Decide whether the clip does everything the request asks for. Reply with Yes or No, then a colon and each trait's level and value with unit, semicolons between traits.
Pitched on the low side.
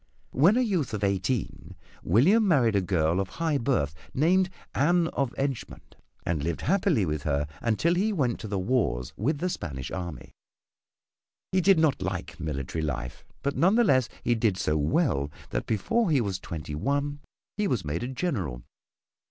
Yes: low, 120 Hz